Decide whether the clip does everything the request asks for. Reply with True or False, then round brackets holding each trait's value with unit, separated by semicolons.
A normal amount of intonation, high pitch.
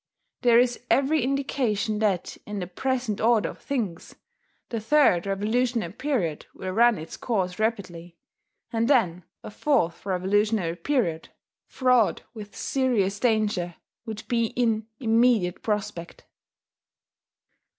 True (4.7 semitones; 215 Hz)